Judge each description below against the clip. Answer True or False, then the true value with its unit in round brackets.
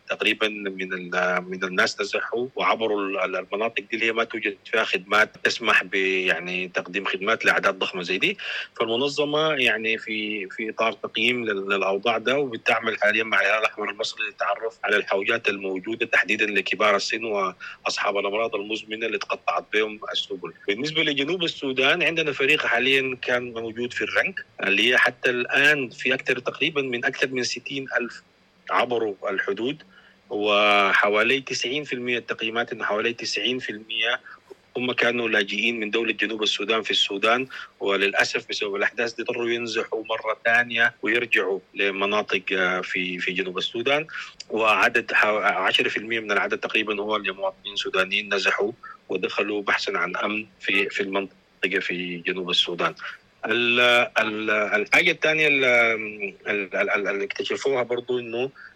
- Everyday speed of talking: False (130 wpm)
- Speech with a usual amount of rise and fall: True (3.5 semitones)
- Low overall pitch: True (115 Hz)